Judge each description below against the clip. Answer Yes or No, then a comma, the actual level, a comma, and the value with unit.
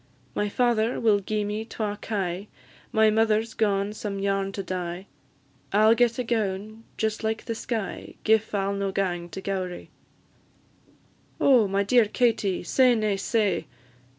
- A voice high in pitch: Yes, high, 210 Hz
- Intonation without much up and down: Yes, narrow, 2.2 semitones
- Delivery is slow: No, average, 160 wpm